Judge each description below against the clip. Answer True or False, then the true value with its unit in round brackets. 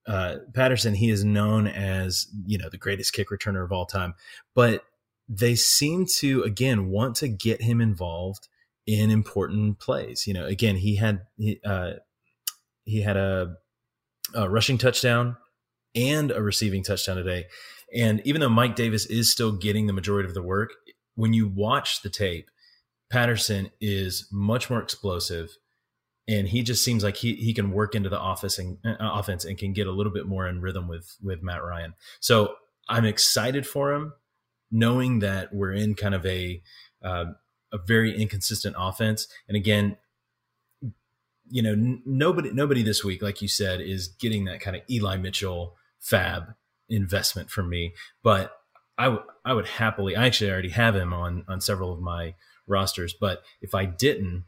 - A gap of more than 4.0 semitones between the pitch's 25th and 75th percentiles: False (3.2 semitones)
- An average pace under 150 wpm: False (175 wpm)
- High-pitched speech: False (105 Hz)